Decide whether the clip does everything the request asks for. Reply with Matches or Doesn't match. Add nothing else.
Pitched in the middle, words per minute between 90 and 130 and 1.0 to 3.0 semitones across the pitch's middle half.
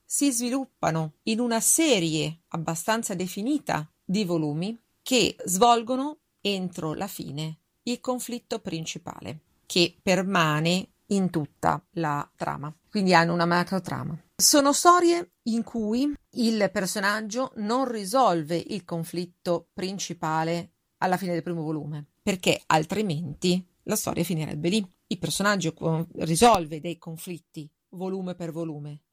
Doesn't match